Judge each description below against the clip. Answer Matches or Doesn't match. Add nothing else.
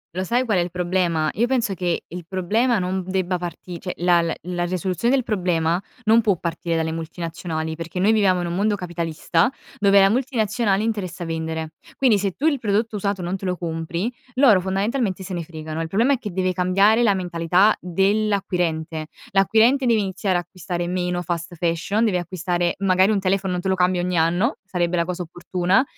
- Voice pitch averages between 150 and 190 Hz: Matches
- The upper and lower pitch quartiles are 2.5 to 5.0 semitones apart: Matches